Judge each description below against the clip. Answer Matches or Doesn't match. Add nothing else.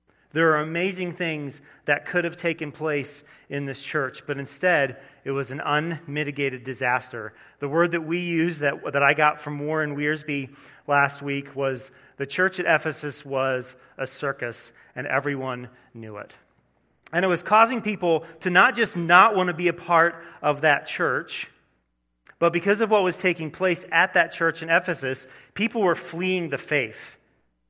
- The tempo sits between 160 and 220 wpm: Matches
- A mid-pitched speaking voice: Matches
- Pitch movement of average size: Matches